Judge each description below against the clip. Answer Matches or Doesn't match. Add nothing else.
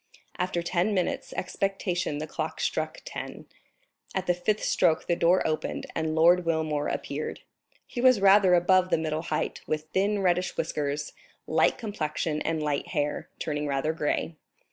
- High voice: Doesn't match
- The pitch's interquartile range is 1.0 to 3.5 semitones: Matches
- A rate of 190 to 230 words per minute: Doesn't match